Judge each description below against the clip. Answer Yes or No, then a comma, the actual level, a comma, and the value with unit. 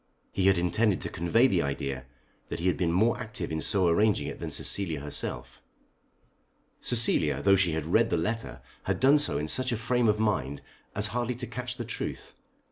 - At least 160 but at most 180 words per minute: No, average, 200 wpm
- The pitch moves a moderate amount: No, wide, 6.3 semitones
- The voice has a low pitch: Yes, low, 100 Hz